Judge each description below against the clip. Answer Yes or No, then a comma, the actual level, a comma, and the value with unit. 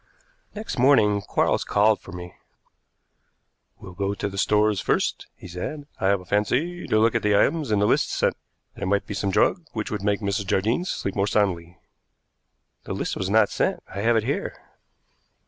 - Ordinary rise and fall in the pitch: No, narrow, 2.3 semitones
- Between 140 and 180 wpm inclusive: No, average, 190 wpm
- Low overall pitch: Yes, low, 105 Hz